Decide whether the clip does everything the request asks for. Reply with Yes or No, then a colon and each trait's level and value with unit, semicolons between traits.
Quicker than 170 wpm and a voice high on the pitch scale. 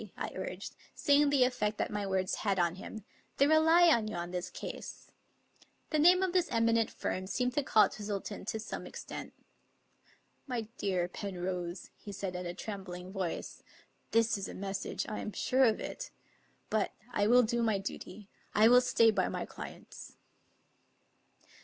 Yes: average, 185 wpm; high, 215 Hz